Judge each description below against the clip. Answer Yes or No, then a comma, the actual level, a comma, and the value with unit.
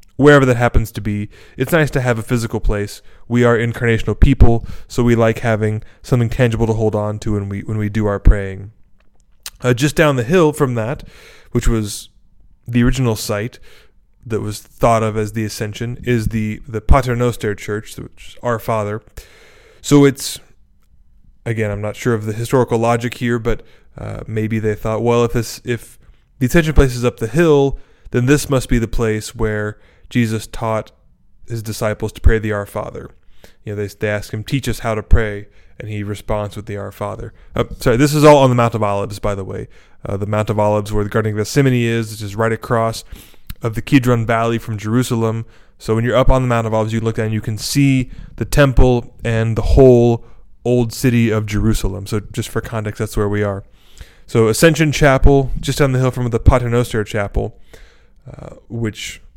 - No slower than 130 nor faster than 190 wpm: No, fast, 205 wpm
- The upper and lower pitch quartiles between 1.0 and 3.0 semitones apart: Yes, narrow, 2.5 semitones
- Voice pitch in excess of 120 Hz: No, low, 115 Hz